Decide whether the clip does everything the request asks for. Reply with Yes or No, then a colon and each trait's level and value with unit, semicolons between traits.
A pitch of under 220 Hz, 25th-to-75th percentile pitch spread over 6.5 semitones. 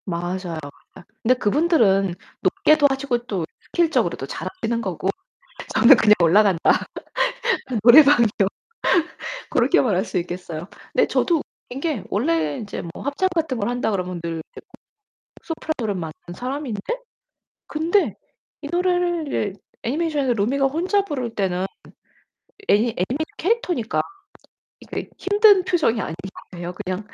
No: high, 235 Hz; wide, 8.5 semitones